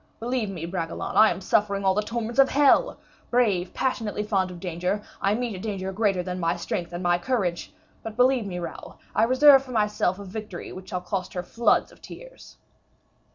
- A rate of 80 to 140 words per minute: No, average, 200 wpm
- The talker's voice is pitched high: Yes, high, 200 Hz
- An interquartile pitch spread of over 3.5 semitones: Yes, average, 4.4 semitones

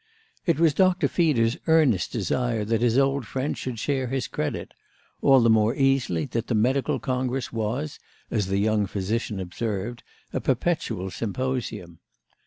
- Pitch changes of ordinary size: Yes, average, 4.0 semitones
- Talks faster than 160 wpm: No, average, 145 wpm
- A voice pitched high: No, low, 120 Hz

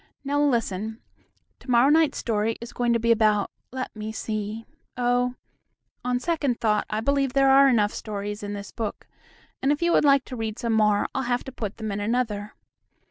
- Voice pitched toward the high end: Yes, high, 230 Hz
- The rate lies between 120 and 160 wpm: No, average, 195 wpm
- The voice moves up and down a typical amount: Yes, average, 3.6 semitones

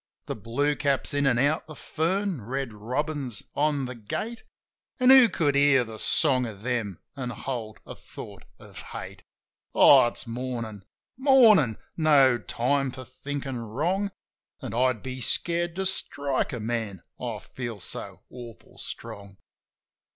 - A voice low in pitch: Yes, low, 130 Hz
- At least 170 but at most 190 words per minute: No, average, 145 wpm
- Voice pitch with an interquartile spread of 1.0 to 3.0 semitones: No, average, 4.3 semitones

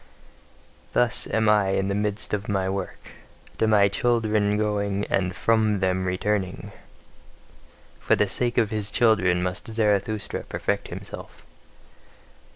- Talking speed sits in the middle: No, slow, 130 wpm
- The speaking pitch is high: No, low, 105 Hz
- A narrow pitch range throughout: Yes, narrow, 2.0 semitones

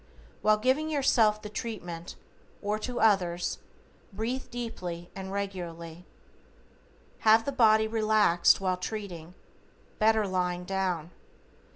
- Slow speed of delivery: Yes, slow, 105 wpm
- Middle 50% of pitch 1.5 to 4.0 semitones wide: Yes, average, 3.7 semitones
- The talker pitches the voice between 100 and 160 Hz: No, high, 205 Hz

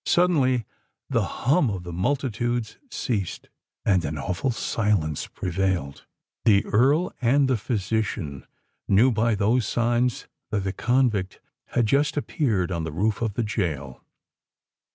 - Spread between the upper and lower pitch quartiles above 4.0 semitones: Yes, average, 5.0 semitones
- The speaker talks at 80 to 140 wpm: Yes, slow, 135 wpm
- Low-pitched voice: Yes, low, 110 Hz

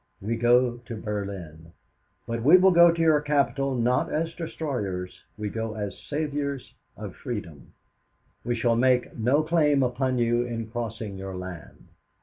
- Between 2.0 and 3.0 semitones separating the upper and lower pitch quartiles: No, average, 5.1 semitones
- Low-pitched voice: Yes, low, 120 Hz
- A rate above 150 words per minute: No, average, 145 wpm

